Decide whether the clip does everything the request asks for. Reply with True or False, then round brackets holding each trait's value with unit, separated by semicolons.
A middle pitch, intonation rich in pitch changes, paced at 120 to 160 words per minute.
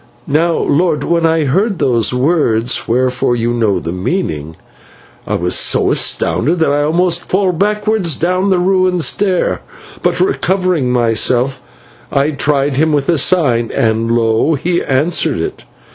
True (150 Hz; 6.7 semitones; 145 wpm)